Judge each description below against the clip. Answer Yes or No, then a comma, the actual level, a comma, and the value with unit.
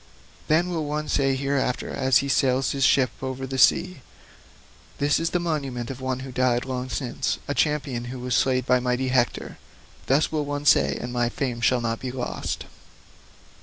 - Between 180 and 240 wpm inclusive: Yes, average, 185 wpm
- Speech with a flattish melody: Yes, narrow, 2.2 semitones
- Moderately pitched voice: No, low, 130 Hz